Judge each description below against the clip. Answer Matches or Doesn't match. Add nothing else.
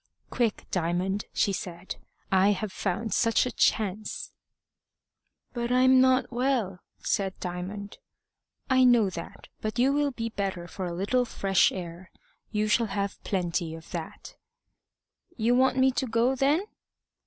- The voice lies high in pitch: Matches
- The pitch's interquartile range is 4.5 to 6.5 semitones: Matches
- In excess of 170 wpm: Doesn't match